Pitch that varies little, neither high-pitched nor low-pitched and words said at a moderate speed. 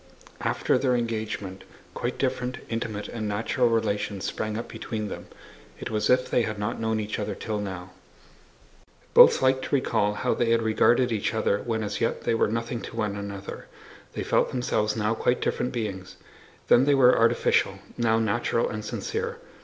No: narrow, 2.3 semitones; low, 110 Hz; average, 180 wpm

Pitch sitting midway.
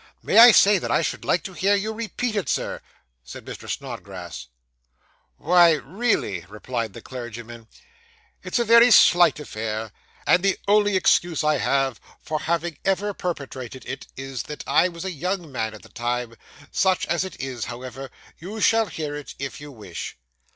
Yes: medium, 155 Hz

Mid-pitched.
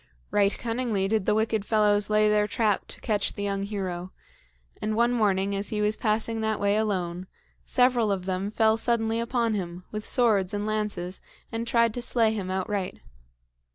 No: high, 210 Hz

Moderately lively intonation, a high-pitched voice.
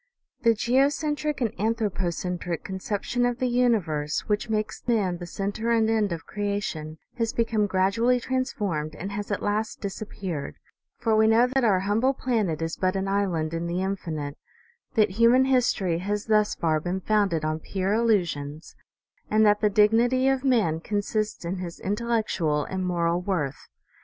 Yes: average, 4.5 semitones; high, 205 Hz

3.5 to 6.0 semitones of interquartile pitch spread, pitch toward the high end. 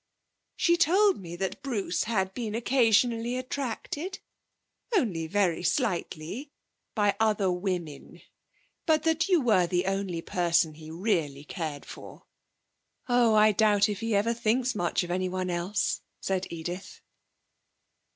Yes: average, 5.2 semitones; high, 205 Hz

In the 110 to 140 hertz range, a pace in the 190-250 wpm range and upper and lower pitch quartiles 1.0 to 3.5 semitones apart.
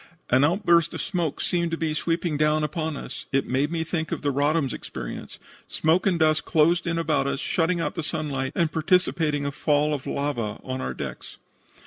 No: medium, 155 Hz; average, 195 wpm; average, 2.7 semitones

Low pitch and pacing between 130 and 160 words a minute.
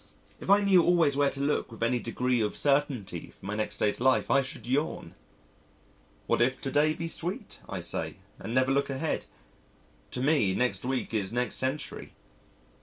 No: low, 130 Hz; average, 180 wpm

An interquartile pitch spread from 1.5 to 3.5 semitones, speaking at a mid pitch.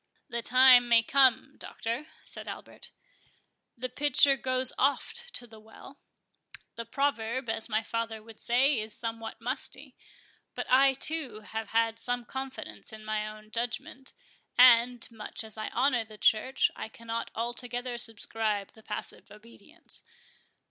No: average, 2.7 semitones; high, 235 Hz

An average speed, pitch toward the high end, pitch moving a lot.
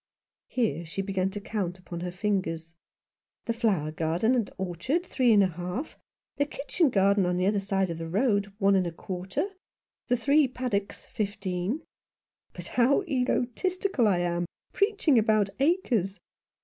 Yes: average, 155 wpm; high, 200 Hz; wide, 5.7 semitones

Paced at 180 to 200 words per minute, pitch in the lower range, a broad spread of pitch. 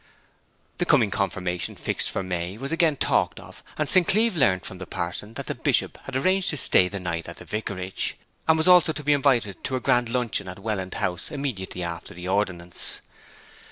Yes: average, 195 wpm; low, 105 Hz; wide, 7.7 semitones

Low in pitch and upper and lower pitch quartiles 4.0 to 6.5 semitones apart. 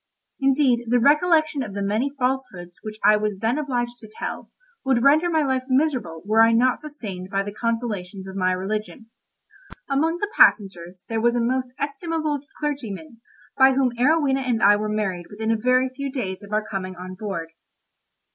No: high, 235 Hz; average, 5.0 semitones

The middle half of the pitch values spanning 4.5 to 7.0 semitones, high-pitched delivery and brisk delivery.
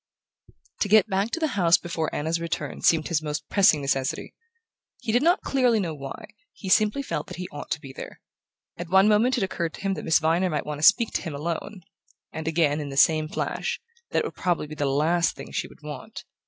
No: average, 4.9 semitones; medium, 170 Hz; fast, 230 wpm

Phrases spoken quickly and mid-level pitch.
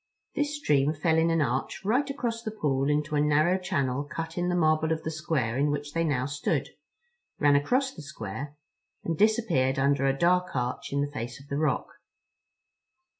No: average, 190 wpm; medium, 150 Hz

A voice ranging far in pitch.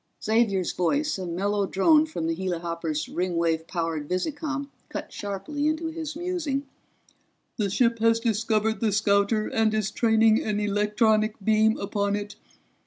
No: average, 3.5 semitones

